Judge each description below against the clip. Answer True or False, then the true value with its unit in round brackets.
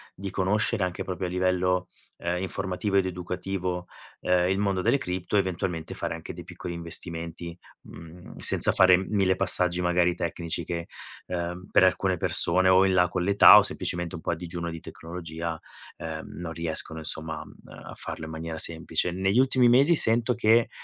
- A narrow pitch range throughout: True (2.0 semitones)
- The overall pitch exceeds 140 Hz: False (90 Hz)